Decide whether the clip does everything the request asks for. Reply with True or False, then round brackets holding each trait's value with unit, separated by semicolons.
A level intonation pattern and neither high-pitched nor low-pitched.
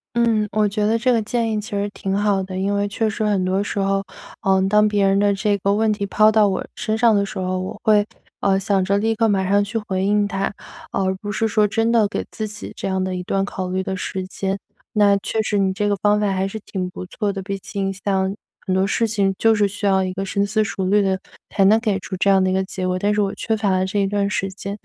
False (1.7 semitones; 200 Hz)